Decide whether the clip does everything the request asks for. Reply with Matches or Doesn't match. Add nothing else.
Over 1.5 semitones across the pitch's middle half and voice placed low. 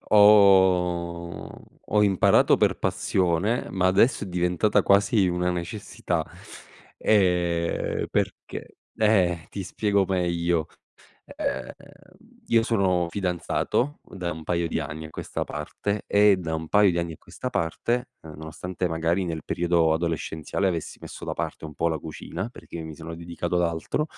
Matches